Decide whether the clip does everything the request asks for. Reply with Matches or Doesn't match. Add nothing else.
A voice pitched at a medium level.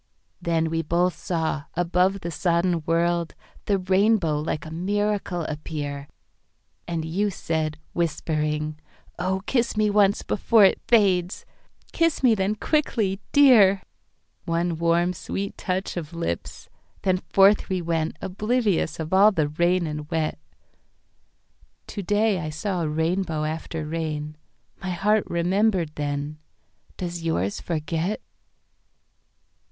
Matches